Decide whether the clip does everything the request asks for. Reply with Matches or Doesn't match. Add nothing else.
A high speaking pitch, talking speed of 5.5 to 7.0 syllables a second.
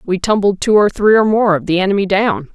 Matches